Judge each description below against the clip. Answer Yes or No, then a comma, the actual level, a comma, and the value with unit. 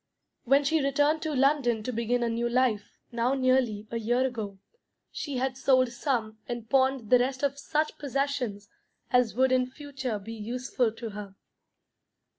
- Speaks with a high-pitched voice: Yes, very high, 255 Hz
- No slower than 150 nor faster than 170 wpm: Yes, average, 165 wpm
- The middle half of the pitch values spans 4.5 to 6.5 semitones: No, average, 3.0 semitones